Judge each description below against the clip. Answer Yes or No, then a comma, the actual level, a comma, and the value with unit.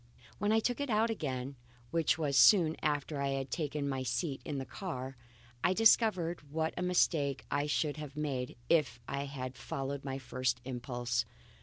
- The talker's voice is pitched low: No, medium, 145 Hz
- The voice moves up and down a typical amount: Yes, average, 3.7 semitones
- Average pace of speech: Yes, average, 175 wpm